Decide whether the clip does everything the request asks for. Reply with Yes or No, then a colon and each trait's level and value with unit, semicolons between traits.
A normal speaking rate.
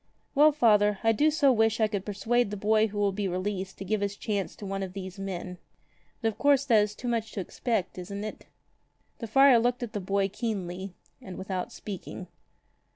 No: fast, 210 wpm